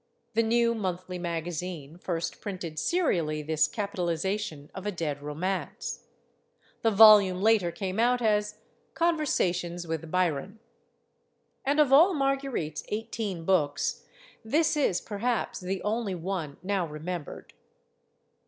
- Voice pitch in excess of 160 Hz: Yes, high, 190 Hz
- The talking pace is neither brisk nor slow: No, slow, 115 wpm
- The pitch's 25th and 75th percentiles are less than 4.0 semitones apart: No, average, 4.9 semitones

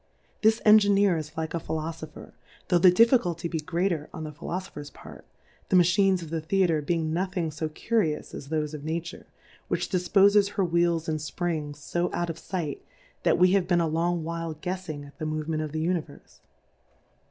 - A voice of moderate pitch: Yes, medium, 170 Hz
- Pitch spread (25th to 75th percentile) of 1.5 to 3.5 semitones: Yes, average, 2.8 semitones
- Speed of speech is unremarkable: Yes, average, 190 wpm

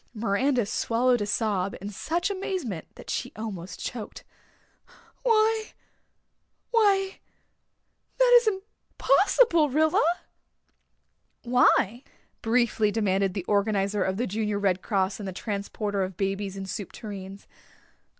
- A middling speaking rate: No, slow, 115 wpm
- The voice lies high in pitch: Yes, high, 215 Hz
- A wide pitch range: Yes, wide, 7.4 semitones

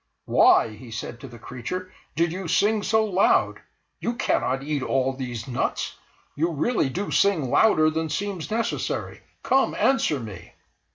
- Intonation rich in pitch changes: Yes, wide, 7.6 semitones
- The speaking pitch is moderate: Yes, medium, 155 Hz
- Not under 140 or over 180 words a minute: Yes, average, 155 wpm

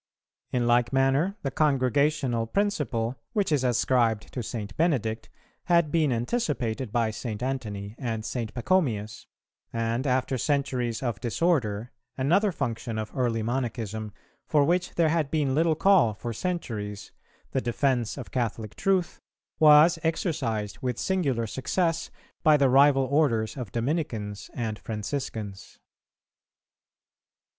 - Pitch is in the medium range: No, low, 130 Hz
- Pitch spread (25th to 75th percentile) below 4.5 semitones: No, average, 5.0 semitones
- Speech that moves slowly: Yes, slow, 125 wpm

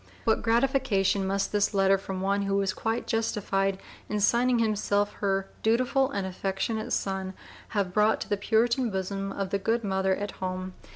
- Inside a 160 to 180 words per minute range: Yes, average, 170 wpm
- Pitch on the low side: No, high, 200 Hz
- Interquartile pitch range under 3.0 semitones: Yes, narrow, 2.5 semitones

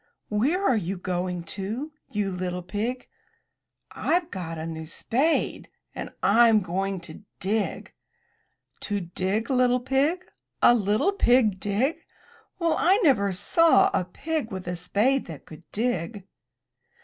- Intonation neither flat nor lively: No, wide, 5.9 semitones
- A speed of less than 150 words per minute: Yes, slow, 135 wpm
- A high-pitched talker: Yes, high, 205 Hz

